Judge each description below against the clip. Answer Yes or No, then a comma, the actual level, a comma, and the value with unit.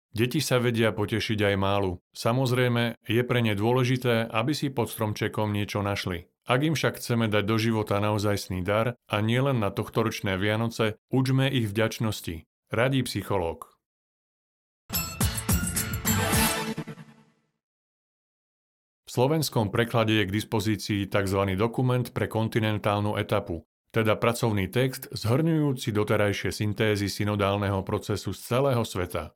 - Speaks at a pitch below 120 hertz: Yes, low, 110 Hz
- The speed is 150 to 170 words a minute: No, average, 120 wpm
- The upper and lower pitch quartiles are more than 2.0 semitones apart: Yes, average, 2.9 semitones